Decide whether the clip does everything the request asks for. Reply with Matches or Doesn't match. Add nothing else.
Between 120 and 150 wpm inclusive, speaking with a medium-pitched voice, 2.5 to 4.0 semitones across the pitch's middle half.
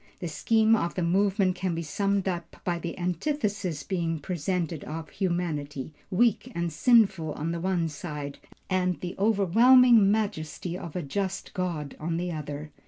Doesn't match